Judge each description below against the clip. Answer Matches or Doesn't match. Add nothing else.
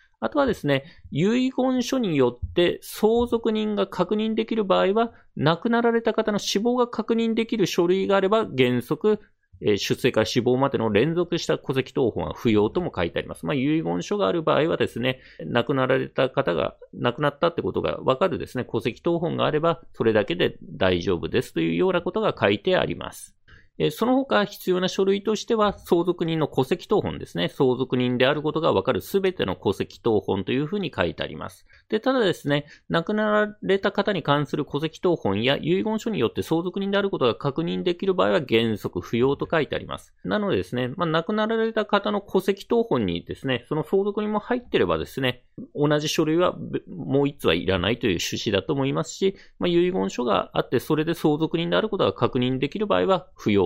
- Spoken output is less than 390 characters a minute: Doesn't match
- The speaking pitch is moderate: Matches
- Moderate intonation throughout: Doesn't match